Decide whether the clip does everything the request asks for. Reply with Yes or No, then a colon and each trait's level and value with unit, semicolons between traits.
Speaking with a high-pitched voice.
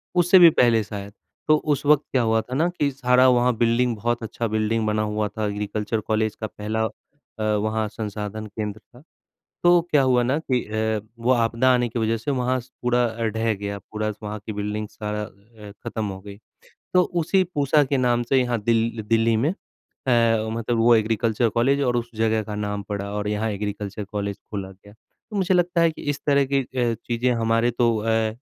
No: low, 115 Hz